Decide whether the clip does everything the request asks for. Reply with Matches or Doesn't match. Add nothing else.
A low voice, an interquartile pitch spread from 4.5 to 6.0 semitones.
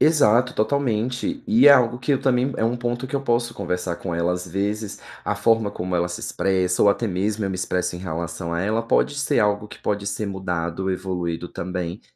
Matches